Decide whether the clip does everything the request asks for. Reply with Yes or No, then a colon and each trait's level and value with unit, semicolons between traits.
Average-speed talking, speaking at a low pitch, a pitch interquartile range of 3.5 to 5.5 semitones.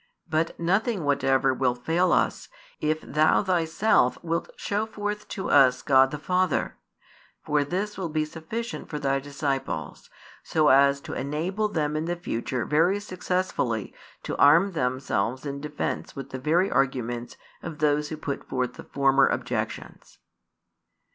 No: average, 150 wpm; medium, 150 Hz; average, 4.4 semitones